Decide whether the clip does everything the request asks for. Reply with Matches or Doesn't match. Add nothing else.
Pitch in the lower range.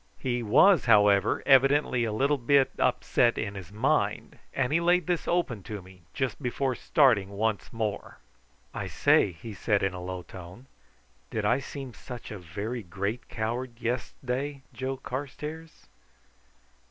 Matches